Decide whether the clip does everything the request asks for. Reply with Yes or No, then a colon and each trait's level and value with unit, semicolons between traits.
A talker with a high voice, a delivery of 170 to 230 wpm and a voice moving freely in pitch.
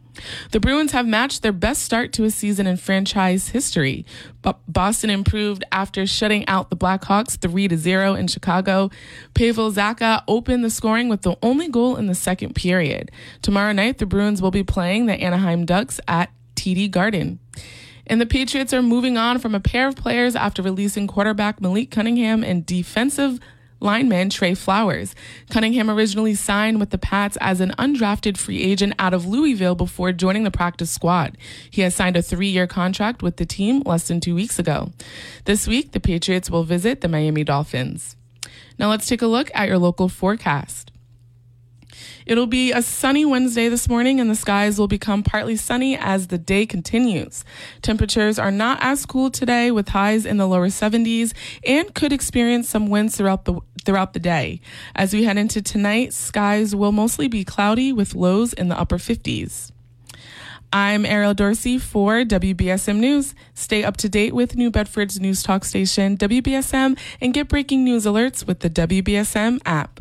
No: high, 205 Hz; average, 175 wpm; average, 4.0 semitones